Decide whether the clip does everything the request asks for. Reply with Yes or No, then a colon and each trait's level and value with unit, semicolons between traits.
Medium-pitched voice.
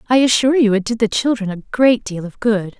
No: high, 225 Hz